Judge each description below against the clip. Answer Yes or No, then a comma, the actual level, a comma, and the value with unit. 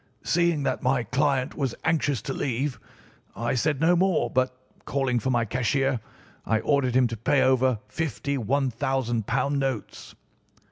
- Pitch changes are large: No, average, 2.7 semitones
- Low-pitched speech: Yes, low, 130 Hz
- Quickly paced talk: No, average, 150 wpm